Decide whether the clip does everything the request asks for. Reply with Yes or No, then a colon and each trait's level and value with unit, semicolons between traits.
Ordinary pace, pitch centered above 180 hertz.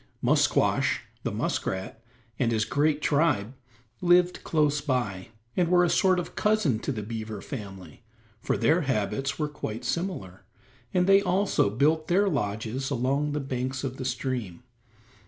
No: average, 150 wpm; low, 135 Hz